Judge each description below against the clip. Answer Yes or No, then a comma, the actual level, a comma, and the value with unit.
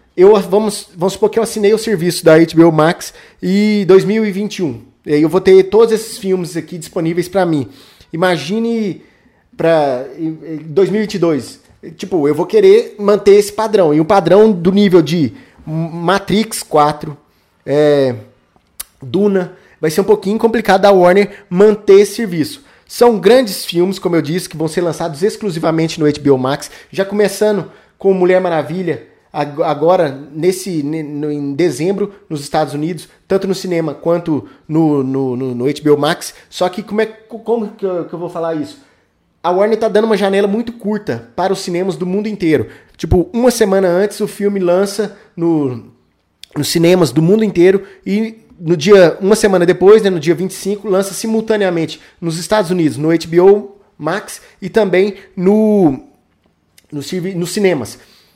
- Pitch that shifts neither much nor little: Yes, average, 4.1 semitones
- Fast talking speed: No, average, 155 wpm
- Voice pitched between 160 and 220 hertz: Yes, medium, 185 Hz